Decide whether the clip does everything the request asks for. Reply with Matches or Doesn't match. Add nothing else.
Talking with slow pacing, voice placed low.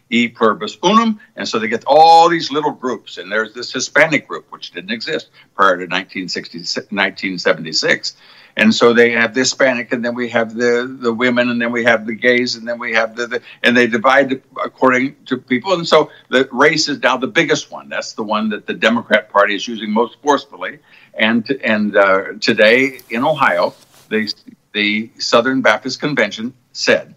Doesn't match